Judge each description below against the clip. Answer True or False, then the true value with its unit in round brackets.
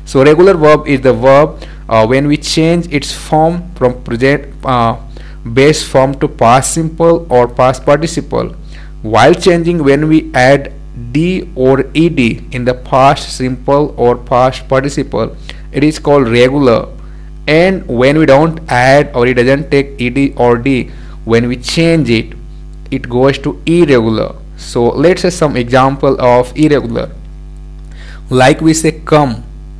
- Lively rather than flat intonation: False (3.5 semitones)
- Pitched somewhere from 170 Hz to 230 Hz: False (140 Hz)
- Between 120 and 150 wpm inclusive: True (145 wpm)